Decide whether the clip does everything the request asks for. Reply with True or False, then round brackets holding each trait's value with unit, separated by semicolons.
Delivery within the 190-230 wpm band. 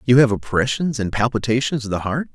True (205 wpm)